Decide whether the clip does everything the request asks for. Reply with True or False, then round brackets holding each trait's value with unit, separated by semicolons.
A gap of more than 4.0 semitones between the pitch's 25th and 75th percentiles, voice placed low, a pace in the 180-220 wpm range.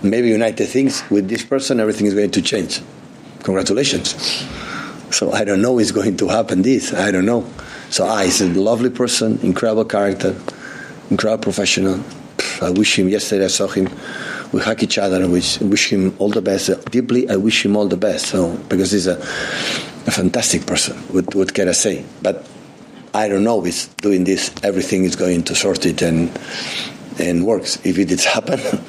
False (3.1 semitones; 100 Hz; 195 wpm)